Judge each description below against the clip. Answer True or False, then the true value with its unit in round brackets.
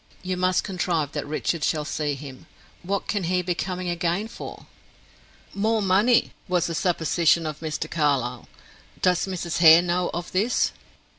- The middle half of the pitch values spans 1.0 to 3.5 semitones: True (2.7 semitones)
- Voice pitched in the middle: True (175 Hz)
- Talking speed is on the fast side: False (155 wpm)